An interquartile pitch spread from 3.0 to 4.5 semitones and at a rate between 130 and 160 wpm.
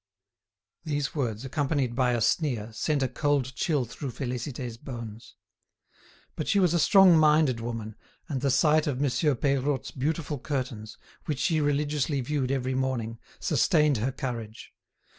Yes: average, 3.5 semitones; average, 145 wpm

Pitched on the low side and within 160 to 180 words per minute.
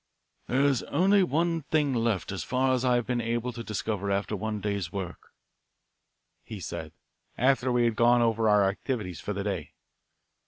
Yes: low, 115 Hz; average, 175 wpm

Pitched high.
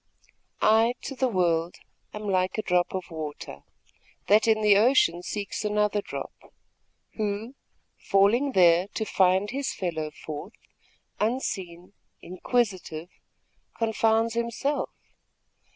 Yes: high, 205 Hz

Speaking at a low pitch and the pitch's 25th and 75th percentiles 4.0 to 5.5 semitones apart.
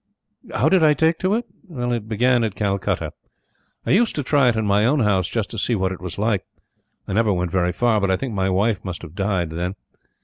Yes: low, 105 Hz; average, 4.5 semitones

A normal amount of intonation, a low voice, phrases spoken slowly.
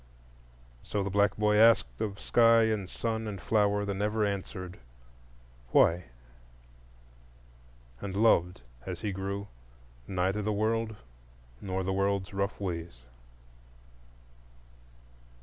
No: narrow, 2.1 semitones; low, 100 Hz; slow, 110 wpm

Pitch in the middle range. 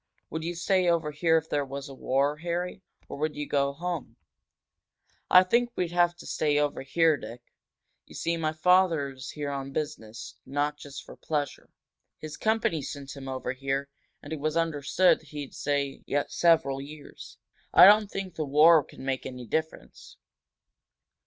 Yes: medium, 150 Hz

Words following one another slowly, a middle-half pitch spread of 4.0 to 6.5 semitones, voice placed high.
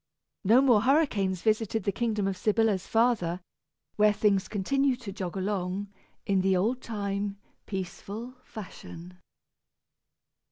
No: slow, 120 wpm; average, 2.8 semitones; high, 205 Hz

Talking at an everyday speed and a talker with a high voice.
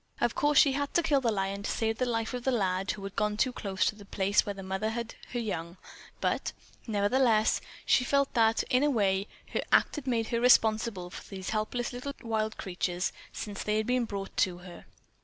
No: fast, 220 wpm; high, 220 Hz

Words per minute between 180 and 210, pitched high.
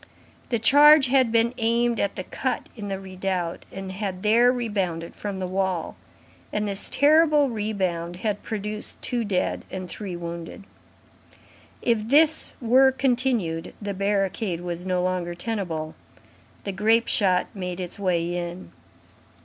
No: average, 140 wpm; high, 200 Hz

